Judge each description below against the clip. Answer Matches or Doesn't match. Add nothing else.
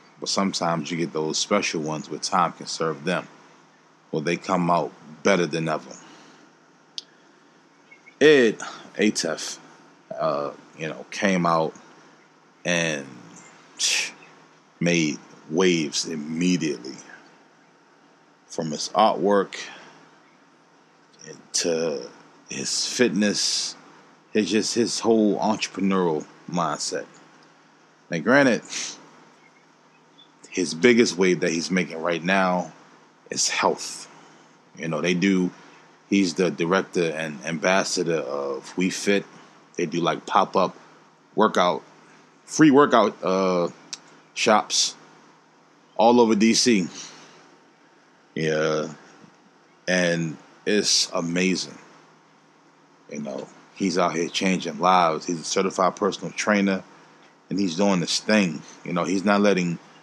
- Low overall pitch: Matches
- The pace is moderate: Doesn't match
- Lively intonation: Doesn't match